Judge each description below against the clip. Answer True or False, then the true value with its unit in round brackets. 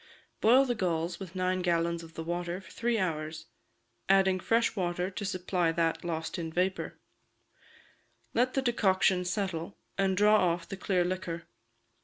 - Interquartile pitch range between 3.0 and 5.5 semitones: False (2.5 semitones)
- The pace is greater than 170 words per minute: False (155 wpm)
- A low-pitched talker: False (185 Hz)